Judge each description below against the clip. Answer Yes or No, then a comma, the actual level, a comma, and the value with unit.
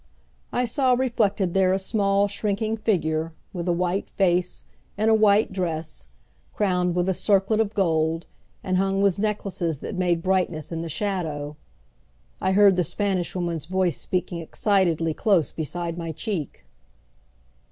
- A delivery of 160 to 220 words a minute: No, average, 150 wpm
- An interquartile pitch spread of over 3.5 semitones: No, average, 3.1 semitones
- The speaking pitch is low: No, medium, 185 Hz